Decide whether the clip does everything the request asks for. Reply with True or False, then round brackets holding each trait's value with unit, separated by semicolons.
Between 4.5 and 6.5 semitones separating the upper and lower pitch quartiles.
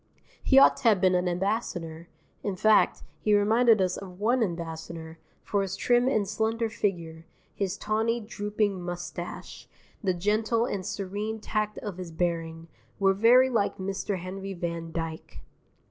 False (3.7 semitones)